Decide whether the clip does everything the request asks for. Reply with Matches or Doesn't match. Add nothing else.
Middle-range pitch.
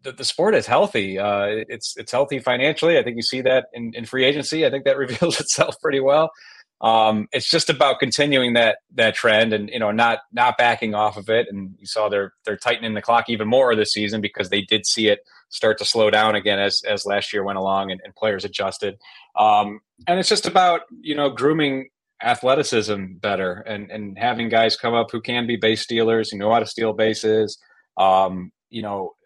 Doesn't match